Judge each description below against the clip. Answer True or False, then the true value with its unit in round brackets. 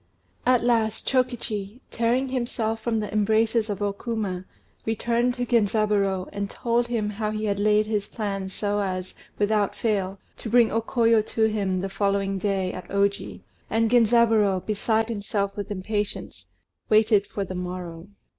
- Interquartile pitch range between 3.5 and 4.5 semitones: False (2.4 semitones)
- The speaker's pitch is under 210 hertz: False (215 Hz)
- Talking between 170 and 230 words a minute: False (155 wpm)